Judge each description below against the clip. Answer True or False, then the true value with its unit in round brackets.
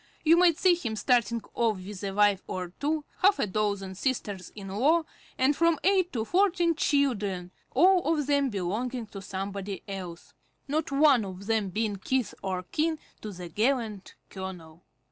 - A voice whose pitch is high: True (220 Hz)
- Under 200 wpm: True (165 wpm)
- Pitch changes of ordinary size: False (7.1 semitones)